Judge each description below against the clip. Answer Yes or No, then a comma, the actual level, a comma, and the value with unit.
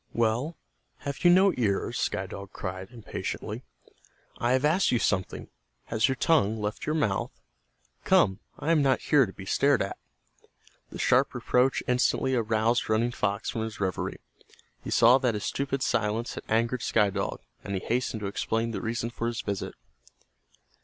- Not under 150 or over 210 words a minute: Yes, average, 170 wpm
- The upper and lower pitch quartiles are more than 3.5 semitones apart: Yes, average, 4.0 semitones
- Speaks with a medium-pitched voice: No, low, 115 Hz